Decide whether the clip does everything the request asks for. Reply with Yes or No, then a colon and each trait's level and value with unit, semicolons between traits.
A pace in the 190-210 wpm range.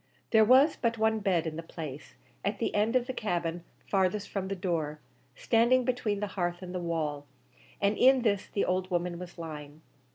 Yes: average, 195 wpm